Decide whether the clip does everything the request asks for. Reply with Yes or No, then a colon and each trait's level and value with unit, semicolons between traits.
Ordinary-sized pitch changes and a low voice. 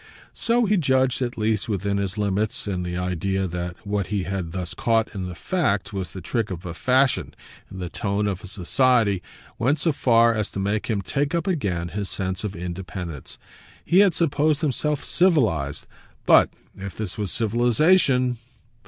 No: wide, 5.7 semitones; low, 105 Hz